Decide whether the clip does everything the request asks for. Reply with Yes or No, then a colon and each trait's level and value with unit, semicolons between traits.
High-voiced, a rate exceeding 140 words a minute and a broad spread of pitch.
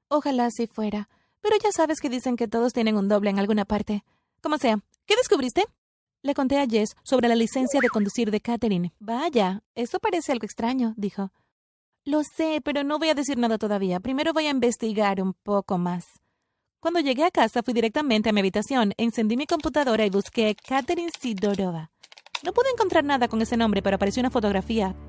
Yes: high, 235 Hz; fast, 190 wpm; wide, 5.7 semitones